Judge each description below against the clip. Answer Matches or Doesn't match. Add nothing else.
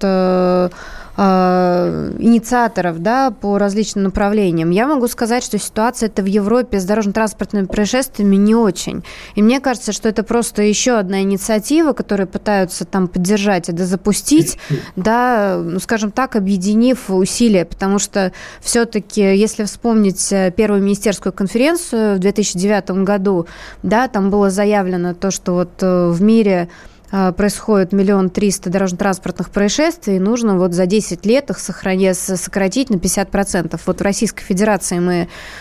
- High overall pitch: Matches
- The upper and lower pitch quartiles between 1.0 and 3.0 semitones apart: Matches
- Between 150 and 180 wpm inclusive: Doesn't match